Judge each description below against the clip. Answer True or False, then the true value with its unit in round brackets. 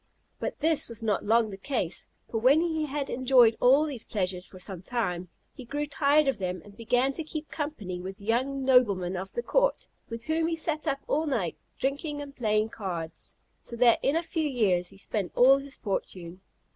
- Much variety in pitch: True (6.6 semitones)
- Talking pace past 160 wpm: True (200 wpm)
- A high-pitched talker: True (245 Hz)